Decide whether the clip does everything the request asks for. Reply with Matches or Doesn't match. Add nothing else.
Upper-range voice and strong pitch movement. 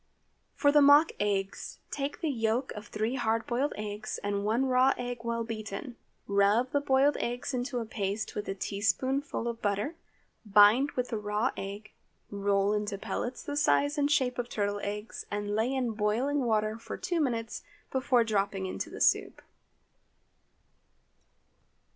Doesn't match